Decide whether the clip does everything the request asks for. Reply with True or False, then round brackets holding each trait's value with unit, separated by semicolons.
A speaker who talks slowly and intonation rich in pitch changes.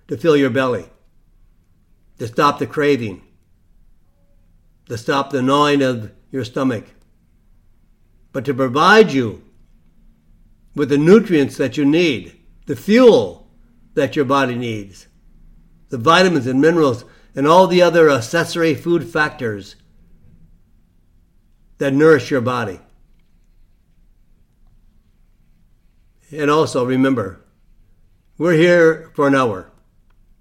True (105 wpm; 8.5 semitones)